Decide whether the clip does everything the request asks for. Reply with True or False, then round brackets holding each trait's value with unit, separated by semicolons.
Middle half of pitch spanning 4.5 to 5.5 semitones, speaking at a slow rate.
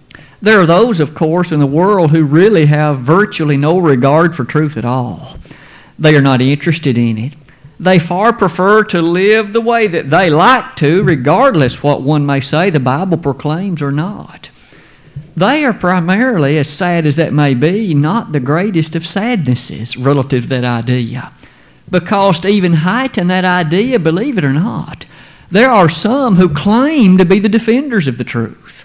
False (5.1 semitones; 175 wpm)